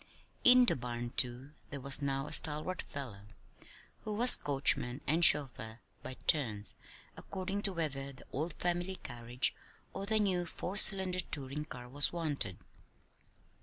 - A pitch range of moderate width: No, wide, 6.0 semitones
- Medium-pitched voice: Yes, medium, 145 Hz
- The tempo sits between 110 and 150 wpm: Yes, average, 145 wpm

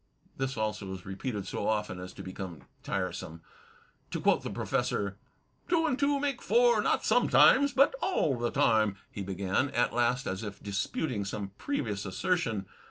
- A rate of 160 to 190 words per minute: Yes, average, 165 wpm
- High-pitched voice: No, low, 105 Hz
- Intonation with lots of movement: Yes, wide, 6.8 semitones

